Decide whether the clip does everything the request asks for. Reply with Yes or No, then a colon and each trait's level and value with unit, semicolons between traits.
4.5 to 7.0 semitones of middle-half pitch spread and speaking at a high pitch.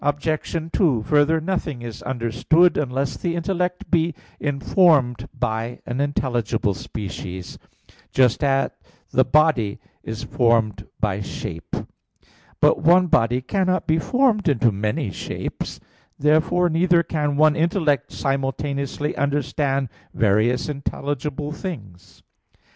No: average, 5.2 semitones; medium, 140 Hz